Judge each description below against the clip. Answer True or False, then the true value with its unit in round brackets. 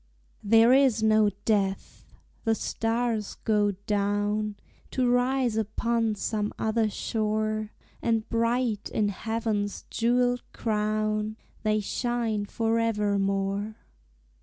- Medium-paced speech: False (100 wpm)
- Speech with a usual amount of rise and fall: False (1.7 semitones)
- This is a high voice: True (215 Hz)